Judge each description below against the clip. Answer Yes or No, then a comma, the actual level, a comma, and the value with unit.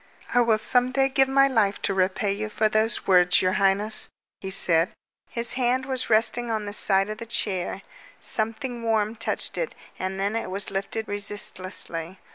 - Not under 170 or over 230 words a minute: Yes, average, 180 wpm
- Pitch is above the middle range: Yes, high, 215 Hz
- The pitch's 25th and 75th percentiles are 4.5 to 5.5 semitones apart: No, average, 3.3 semitones